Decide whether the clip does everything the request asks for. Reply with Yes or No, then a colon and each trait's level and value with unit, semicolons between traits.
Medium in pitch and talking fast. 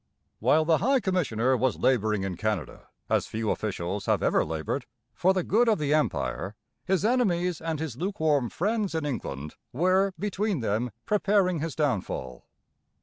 No: medium, 155 Hz; average, 155 wpm